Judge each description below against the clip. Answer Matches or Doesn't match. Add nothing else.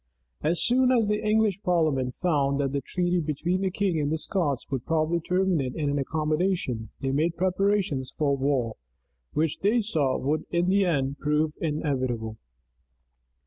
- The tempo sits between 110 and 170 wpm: Matches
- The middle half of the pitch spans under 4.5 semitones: Doesn't match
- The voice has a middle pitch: Matches